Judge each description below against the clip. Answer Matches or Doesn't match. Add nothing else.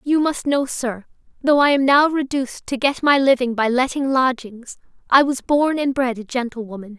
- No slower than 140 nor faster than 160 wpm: Doesn't match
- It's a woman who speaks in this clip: Matches